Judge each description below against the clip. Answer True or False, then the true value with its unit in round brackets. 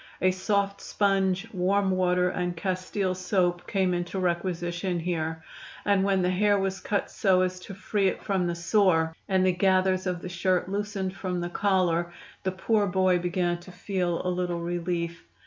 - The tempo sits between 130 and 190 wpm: True (175 wpm)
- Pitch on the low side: False (185 Hz)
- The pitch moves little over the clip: True (1.6 semitones)